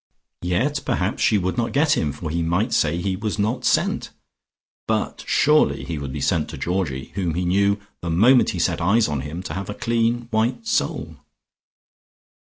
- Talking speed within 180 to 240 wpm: Yes, average, 185 wpm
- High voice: No, very low, 95 Hz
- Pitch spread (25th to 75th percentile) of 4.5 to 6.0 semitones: Yes, wide, 5.4 semitones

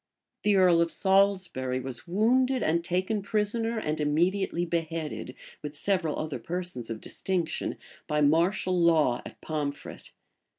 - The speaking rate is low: Yes, slow, 130 wpm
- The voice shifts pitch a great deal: No, average, 4.4 semitones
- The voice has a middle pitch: Yes, medium, 170 Hz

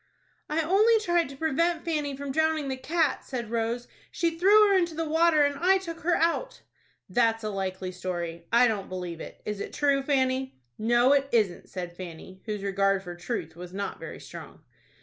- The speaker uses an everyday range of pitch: No, wide, 8.7 semitones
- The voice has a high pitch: Yes, very high, 260 Hz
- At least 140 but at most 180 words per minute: No, average, 190 wpm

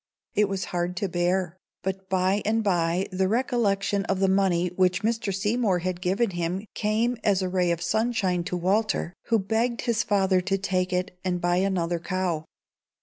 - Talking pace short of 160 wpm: No, average, 180 wpm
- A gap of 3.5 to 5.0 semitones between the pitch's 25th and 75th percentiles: No, narrow, 2.5 semitones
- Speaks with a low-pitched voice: No, high, 190 Hz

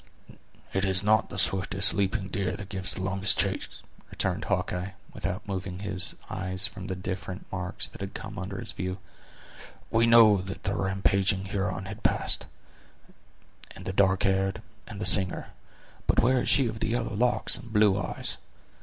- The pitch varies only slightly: Yes, narrow, 1.8 semitones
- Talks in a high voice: No, very low, 95 Hz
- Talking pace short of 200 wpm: Yes, average, 170 wpm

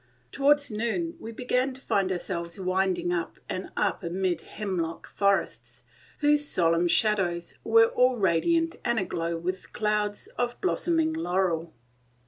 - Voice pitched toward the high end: Yes, high, 195 Hz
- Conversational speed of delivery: No, slow, 130 wpm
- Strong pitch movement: Yes, wide, 6.4 semitones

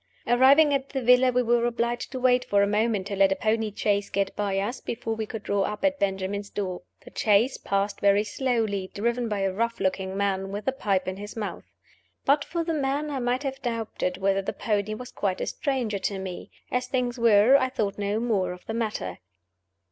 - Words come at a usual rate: No, fast, 215 wpm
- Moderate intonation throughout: Yes, average, 3.9 semitones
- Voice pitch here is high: Yes, high, 215 Hz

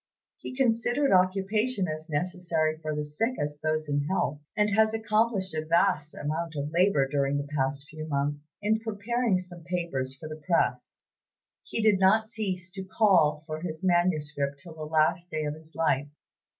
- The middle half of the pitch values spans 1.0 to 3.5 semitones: No, average, 4.6 semitones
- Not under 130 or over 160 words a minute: No, average, 175 wpm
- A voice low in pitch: No, medium, 165 Hz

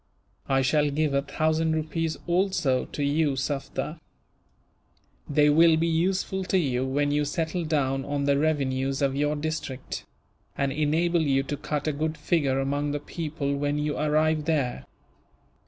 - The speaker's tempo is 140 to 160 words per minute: Yes, average, 155 wpm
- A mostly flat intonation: Yes, narrow, 2.2 semitones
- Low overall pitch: No, medium, 150 Hz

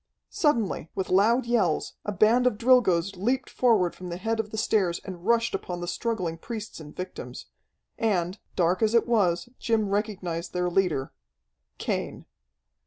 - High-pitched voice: Yes, high, 200 Hz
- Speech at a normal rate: Yes, average, 160 wpm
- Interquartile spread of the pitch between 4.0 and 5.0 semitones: Yes, average, 4.3 semitones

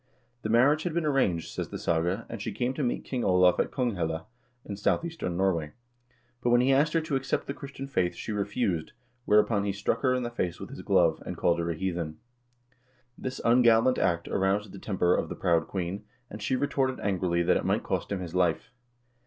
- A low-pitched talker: Yes, low, 105 Hz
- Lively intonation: Yes, wide, 6.3 semitones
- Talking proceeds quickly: Yes, fast, 215 wpm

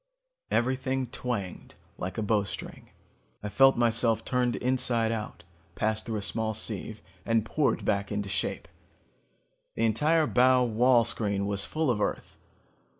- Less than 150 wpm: Yes, average, 140 wpm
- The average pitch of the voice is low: Yes, low, 115 Hz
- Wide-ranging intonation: No, average, 3.3 semitones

